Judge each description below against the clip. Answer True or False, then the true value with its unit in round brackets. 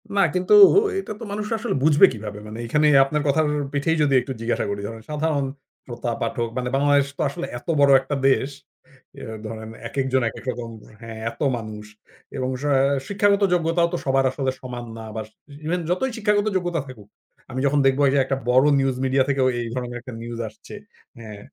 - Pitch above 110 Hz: True (135 Hz)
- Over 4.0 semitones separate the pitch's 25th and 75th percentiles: True (4.7 semitones)